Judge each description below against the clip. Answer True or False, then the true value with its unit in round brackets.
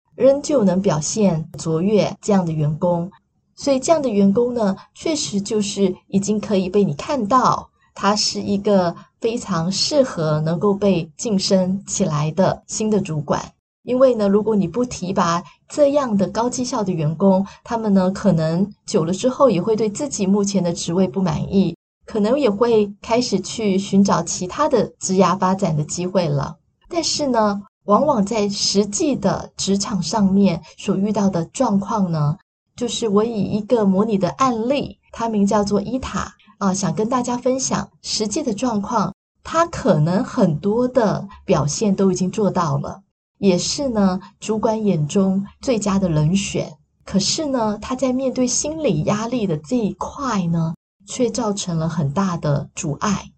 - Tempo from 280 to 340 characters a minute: False (240 characters per minute)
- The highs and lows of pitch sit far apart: False (3.7 semitones)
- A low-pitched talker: False (200 Hz)